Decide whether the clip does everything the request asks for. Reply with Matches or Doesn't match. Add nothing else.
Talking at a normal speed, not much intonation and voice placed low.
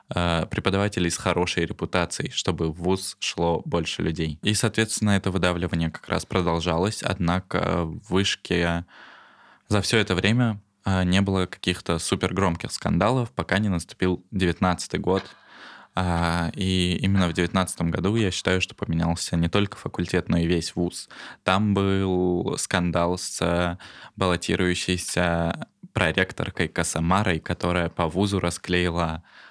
Matches